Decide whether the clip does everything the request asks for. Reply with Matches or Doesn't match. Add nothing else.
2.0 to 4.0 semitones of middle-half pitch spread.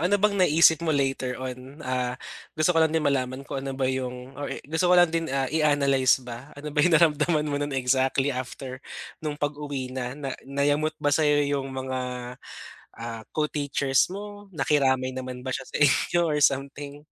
Matches